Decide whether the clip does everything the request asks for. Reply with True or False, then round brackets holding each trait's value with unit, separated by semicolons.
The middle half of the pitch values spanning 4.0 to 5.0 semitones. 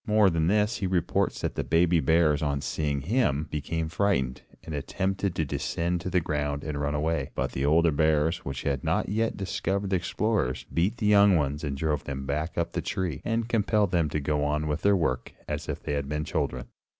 True (4.6 semitones)